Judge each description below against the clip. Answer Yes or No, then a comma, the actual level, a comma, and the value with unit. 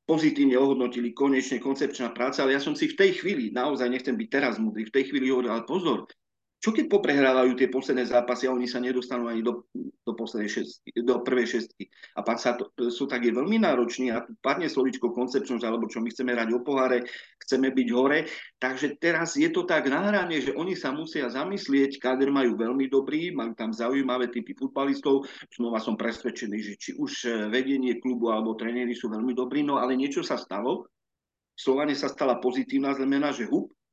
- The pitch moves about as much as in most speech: No, narrow, 2.3 semitones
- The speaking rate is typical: No, fast, 190 wpm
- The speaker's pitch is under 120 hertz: No, low, 130 Hz